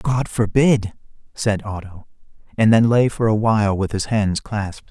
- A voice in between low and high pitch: No, low, 105 Hz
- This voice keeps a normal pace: Yes, average, 170 wpm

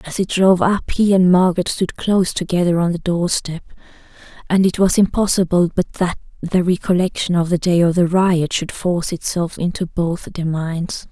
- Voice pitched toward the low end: No, medium, 175 Hz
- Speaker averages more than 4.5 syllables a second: Yes, 5.1 syllables/s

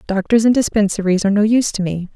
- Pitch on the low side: No, high, 205 Hz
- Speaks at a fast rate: Yes, fast, 225 wpm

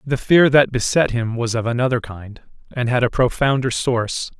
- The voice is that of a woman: No, male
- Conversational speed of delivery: Yes, average, 190 wpm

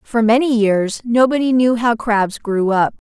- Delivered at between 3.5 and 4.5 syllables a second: Yes, 4.2 syllables/s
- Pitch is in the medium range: No, high, 230 Hz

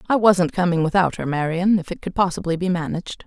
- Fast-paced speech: Yes, fast, 220 wpm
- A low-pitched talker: No, medium, 175 Hz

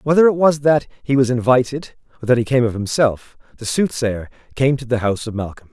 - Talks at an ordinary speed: No, fast, 220 wpm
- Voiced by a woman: No, male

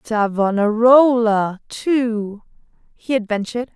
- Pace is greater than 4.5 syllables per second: No, 3.6 syllables/s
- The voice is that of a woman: Yes, female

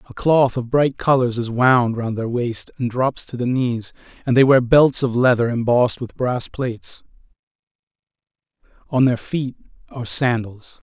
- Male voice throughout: Yes, male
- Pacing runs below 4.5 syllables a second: No, 4.6 syllables/s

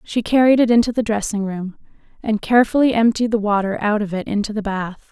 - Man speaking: No, female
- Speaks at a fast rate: Yes, fast, 210 wpm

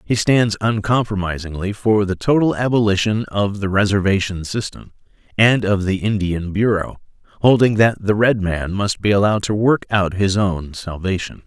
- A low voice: Yes, low, 100 Hz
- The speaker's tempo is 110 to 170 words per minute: Yes, average, 155 wpm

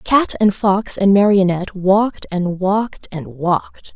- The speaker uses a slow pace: No, average, 150 wpm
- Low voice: No, high, 195 Hz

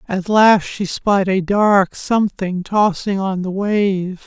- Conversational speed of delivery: Yes, average, 155 wpm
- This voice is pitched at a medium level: No, high, 195 Hz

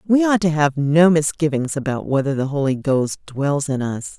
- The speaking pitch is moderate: Yes, medium, 150 Hz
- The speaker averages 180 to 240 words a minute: Yes, average, 200 wpm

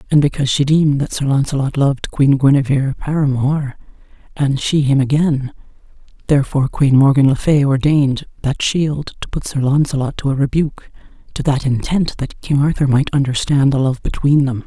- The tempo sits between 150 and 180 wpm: Yes, average, 170 wpm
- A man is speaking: No, female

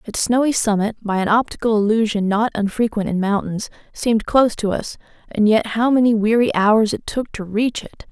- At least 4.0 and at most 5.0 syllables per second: No, 5.3 syllables/s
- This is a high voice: Yes, high, 220 Hz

